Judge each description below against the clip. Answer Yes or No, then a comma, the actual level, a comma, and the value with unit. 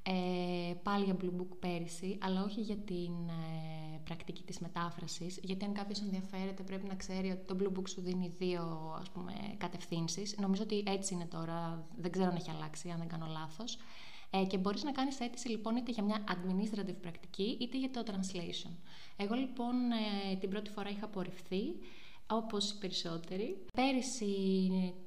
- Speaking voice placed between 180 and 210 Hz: Yes, high, 190 Hz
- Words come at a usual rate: No, fast, 175 wpm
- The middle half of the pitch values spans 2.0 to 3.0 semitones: Yes, narrow, 2.6 semitones